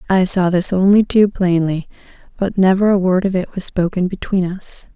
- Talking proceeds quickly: No, average, 195 wpm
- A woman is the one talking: Yes, female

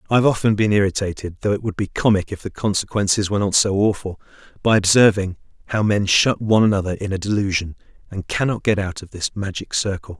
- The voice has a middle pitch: No, low, 100 Hz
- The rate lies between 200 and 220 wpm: Yes, fast, 205 wpm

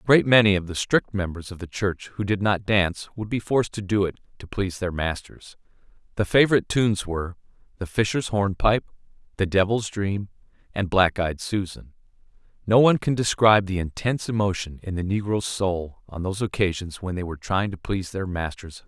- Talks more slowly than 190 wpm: No, average, 195 wpm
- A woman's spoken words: No, male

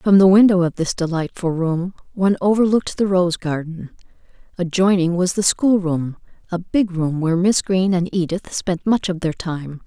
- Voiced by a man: No, female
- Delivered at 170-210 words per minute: Yes, average, 175 wpm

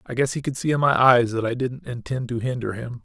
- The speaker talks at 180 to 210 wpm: No, fast, 295 wpm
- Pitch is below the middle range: Yes, low, 125 Hz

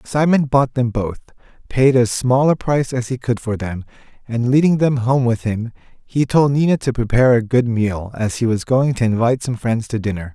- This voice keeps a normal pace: No, fast, 220 wpm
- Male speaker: Yes, male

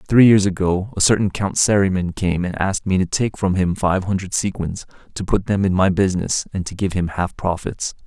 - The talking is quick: Yes, fast, 225 wpm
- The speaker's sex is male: Yes, male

